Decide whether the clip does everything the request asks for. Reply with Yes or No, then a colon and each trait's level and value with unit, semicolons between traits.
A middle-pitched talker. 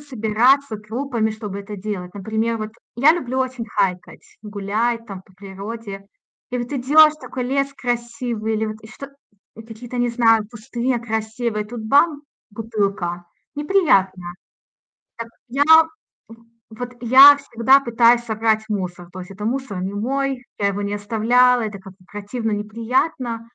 No: high, 225 Hz